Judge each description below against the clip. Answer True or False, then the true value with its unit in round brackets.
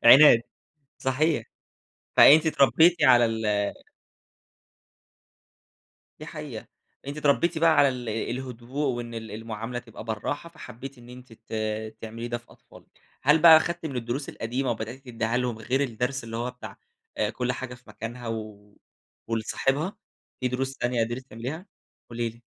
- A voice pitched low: True (125 Hz)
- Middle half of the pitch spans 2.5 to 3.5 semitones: True (3.2 semitones)